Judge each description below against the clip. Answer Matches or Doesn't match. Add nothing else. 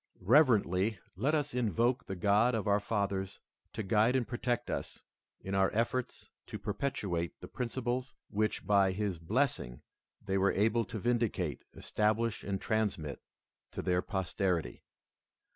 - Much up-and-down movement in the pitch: Doesn't match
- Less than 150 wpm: Matches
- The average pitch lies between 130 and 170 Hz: Doesn't match